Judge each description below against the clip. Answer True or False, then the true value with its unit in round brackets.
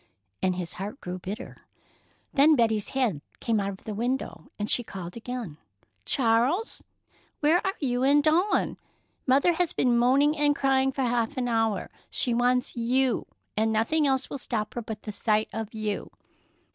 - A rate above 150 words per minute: True (170 wpm)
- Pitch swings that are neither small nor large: True (4.0 semitones)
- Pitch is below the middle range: False (240 Hz)